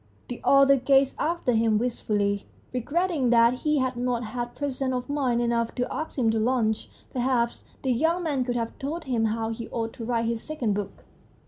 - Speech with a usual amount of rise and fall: Yes, average, 3.0 semitones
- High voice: Yes, high, 245 Hz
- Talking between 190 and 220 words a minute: Yes, average, 195 wpm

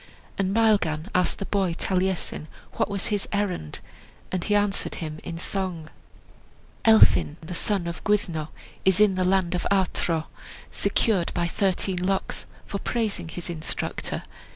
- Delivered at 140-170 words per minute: Yes, average, 145 wpm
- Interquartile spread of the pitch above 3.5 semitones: No, average, 2.9 semitones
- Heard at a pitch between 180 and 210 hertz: Yes, medium, 185 Hz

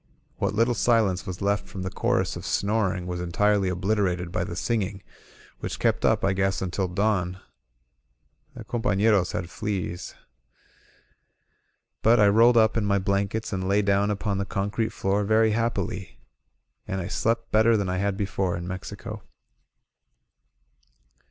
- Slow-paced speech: No, average, 150 wpm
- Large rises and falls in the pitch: No, narrow, 2.5 semitones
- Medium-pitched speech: No, low, 100 Hz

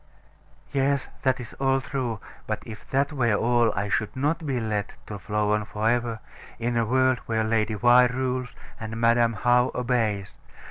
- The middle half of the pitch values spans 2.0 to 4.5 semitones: Yes, average, 2.9 semitones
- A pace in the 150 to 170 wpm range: No, average, 180 wpm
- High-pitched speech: No, low, 120 Hz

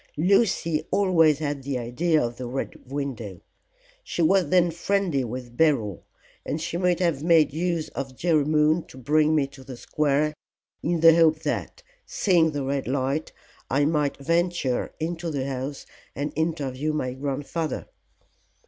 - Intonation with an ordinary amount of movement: Yes, average, 3.6 semitones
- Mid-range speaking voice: Yes, medium, 150 Hz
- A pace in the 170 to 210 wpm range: No, average, 155 wpm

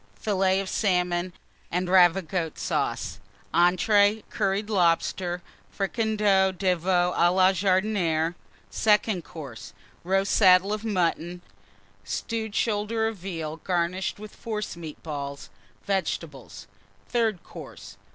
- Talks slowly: Yes, slow, 105 wpm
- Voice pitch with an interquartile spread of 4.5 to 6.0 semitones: No, average, 2.9 semitones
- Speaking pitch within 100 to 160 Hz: No, medium, 185 Hz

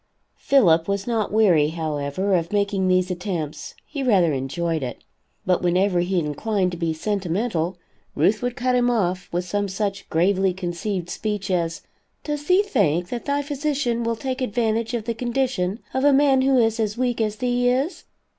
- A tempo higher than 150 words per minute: Yes, average, 175 wpm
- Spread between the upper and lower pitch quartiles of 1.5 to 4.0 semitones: No, wide, 5.6 semitones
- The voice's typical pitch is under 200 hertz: No, high, 205 Hz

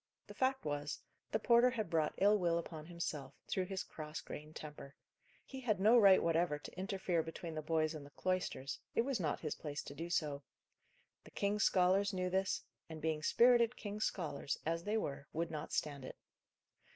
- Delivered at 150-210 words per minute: Yes, average, 190 wpm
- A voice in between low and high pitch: Yes, medium, 170 Hz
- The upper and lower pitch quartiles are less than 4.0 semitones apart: No, average, 4.7 semitones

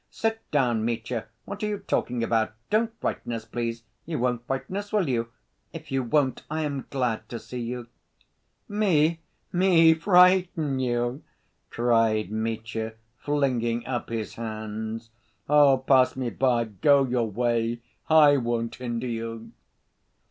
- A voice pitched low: Yes, low, 125 Hz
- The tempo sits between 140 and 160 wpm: Yes, average, 145 wpm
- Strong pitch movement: No, average, 4.3 semitones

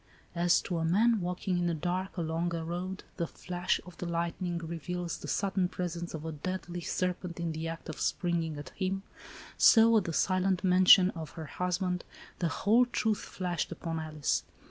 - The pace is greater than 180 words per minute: Yes, average, 190 wpm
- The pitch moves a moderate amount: No, narrow, 2.0 semitones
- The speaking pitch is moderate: Yes, medium, 175 Hz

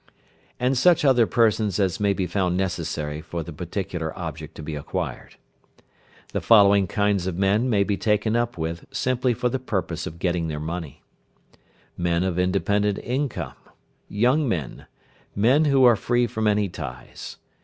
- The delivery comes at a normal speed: Yes, average, 160 wpm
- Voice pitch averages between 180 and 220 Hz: No, low, 100 Hz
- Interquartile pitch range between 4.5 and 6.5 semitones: Yes, wide, 5.4 semitones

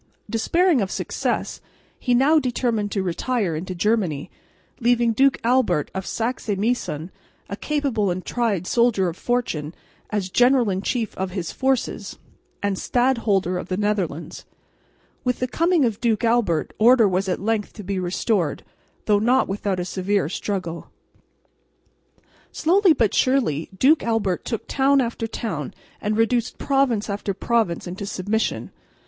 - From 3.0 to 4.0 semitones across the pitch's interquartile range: No, average, 4.7 semitones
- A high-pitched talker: Yes, high, 215 Hz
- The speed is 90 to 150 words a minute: Yes, average, 145 wpm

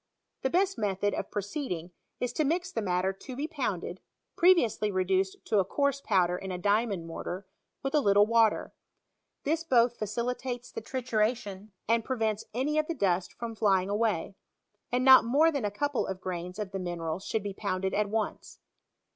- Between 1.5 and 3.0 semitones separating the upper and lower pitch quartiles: No, average, 5.1 semitones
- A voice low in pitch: No, high, 215 Hz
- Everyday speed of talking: Yes, average, 180 wpm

